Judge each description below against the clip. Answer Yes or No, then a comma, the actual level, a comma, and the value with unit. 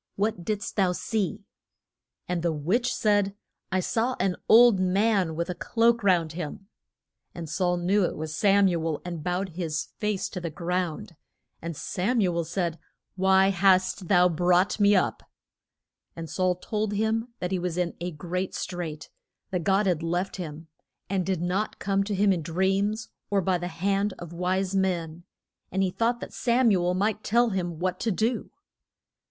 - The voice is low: No, medium, 185 Hz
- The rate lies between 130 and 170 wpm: No, average, 180 wpm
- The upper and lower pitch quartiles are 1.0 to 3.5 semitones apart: Yes, narrow, 2.6 semitones